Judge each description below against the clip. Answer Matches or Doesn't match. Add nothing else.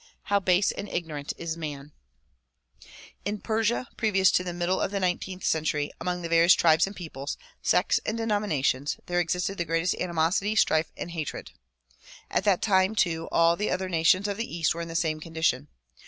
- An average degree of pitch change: Matches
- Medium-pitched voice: Matches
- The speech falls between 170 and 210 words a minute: Matches